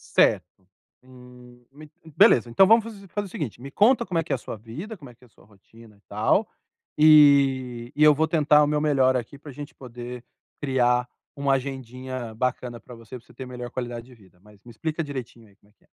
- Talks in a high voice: No, low, 130 Hz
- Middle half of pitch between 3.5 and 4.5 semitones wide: Yes, average, 3.8 semitones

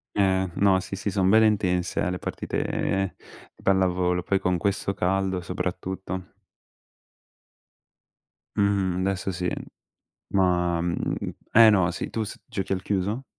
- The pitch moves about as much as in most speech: No, narrow, 1.5 semitones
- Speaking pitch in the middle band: No, very low, 95 Hz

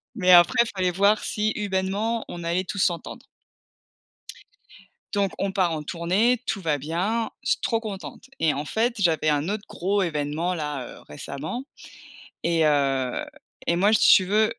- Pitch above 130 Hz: Yes, medium, 185 Hz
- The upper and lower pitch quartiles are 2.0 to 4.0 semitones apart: No, average, 4.7 semitones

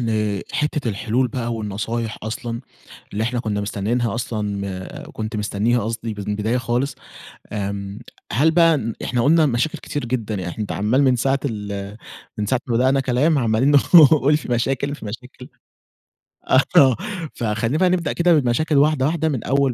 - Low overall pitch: Yes, low, 120 Hz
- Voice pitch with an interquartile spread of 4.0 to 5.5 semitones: Yes, average, 4.5 semitones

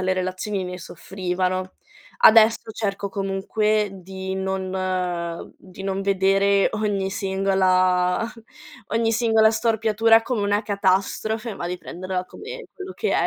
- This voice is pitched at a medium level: No, high, 195 Hz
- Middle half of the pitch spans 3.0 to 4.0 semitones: No, narrow, 2.6 semitones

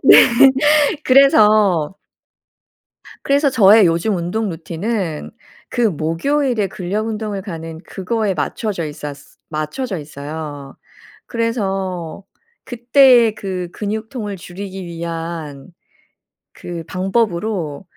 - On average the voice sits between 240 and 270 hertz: No, high, 190 Hz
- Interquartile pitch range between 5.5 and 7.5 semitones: No, average, 5.1 semitones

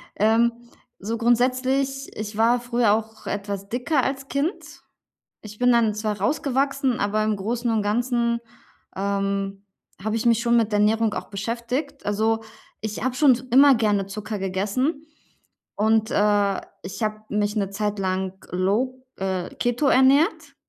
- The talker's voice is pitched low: No, high, 220 Hz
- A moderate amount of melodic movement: Yes, average, 3.3 semitones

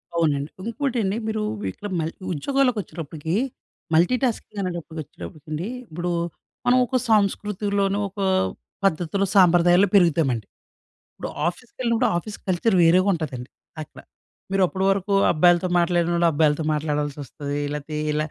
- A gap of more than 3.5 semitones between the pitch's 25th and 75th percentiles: Yes, average, 4.6 semitones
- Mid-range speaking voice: Yes, medium, 175 Hz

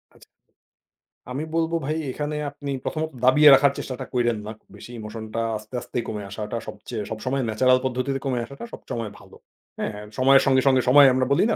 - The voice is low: Yes, low, 130 Hz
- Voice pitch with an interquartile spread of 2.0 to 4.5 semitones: Yes, average, 3.4 semitones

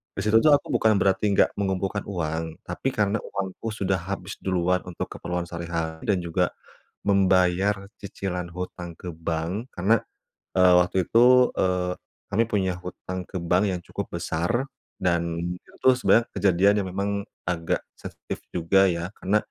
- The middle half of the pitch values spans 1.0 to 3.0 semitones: Yes, narrow, 2.5 semitones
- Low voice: Yes, very low, 95 Hz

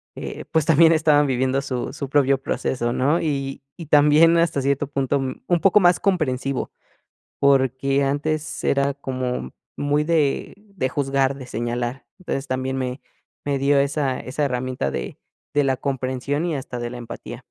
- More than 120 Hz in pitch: Yes, medium, 140 Hz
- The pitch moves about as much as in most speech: No, narrow, 2.3 semitones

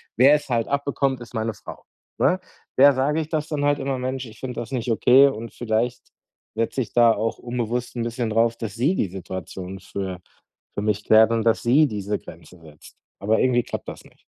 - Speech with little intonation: No, average, 3.4 semitones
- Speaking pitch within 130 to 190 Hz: No, low, 120 Hz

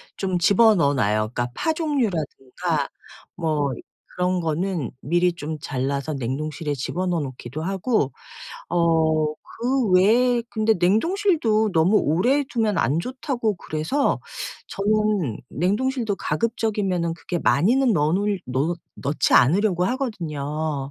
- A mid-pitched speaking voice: Yes, medium, 175 Hz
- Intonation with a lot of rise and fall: Yes, wide, 6.2 semitones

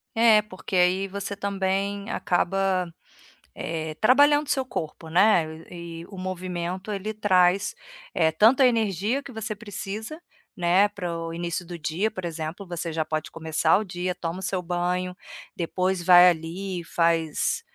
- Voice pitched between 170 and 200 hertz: Yes, medium, 185 Hz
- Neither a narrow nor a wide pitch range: Yes, average, 3.0 semitones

